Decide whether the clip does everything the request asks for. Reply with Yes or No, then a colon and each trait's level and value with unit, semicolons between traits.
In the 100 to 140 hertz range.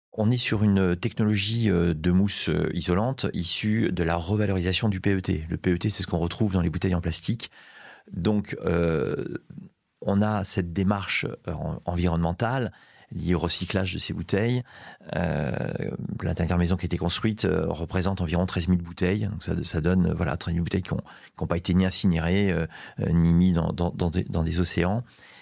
No: very low, 90 Hz